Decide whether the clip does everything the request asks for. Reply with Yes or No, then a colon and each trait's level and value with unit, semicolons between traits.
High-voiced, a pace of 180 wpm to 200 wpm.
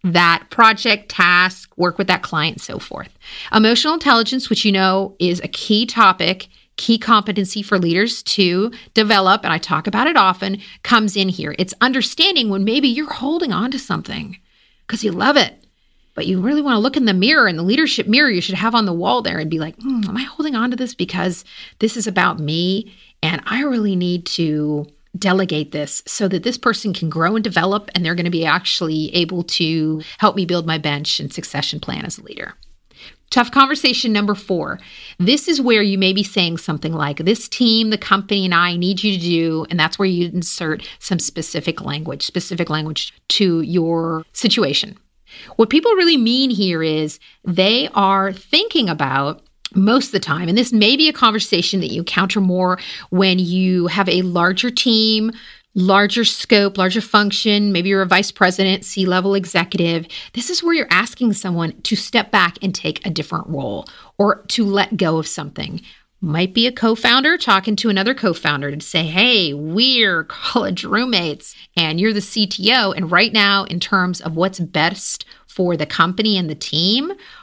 Yes: high, 195 Hz; average, 190 wpm